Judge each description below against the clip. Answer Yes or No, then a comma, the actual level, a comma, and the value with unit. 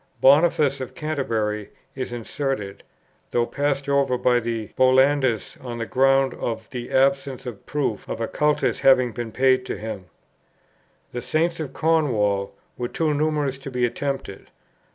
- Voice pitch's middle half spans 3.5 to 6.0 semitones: No, average, 3.1 semitones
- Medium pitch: No, low, 130 Hz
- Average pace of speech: Yes, average, 150 wpm